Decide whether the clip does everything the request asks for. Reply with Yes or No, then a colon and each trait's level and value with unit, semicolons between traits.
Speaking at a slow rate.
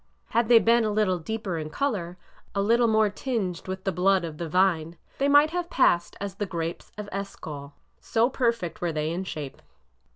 No: average, 195 wpm